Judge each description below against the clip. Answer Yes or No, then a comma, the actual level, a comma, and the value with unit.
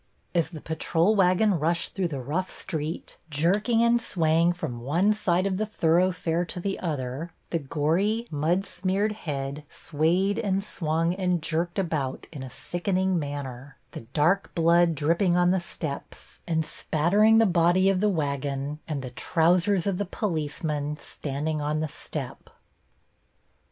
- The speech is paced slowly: No, average, 150 wpm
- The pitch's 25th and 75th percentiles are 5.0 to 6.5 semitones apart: No, average, 3.8 semitones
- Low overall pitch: No, medium, 170 Hz